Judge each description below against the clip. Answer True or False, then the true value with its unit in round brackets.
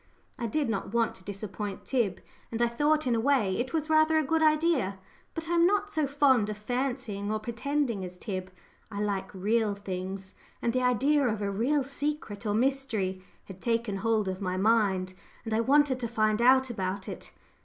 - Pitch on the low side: False (230 Hz)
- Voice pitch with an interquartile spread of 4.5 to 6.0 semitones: True (5.5 semitones)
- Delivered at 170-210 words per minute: True (195 wpm)